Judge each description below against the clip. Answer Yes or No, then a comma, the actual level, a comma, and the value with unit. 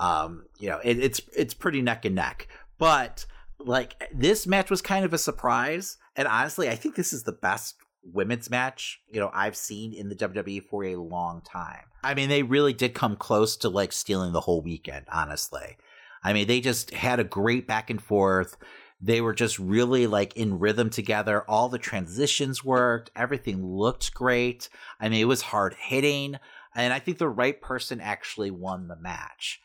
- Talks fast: No, average, 190 wpm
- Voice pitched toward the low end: Yes, low, 115 Hz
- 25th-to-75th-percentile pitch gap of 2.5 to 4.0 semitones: No, average, 4.4 semitones